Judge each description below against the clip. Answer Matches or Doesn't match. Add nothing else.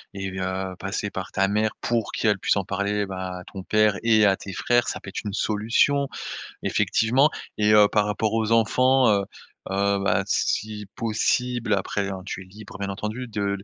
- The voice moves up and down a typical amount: Doesn't match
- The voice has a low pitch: Matches